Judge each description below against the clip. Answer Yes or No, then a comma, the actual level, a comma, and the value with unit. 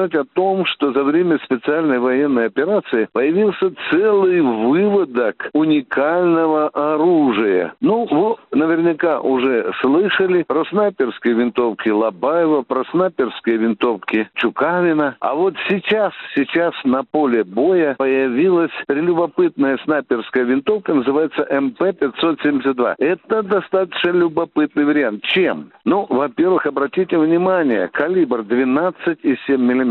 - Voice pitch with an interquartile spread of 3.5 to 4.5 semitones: No, wide, 5.5 semitones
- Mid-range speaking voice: Yes, medium, 155 Hz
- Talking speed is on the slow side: Yes, slow, 100 wpm